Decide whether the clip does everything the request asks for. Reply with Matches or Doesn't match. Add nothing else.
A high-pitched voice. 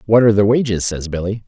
Doesn't match